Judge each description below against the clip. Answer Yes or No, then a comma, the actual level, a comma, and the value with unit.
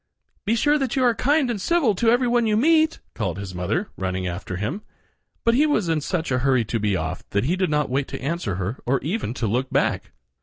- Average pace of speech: No, fast, 240 wpm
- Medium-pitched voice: Yes, medium, 155 Hz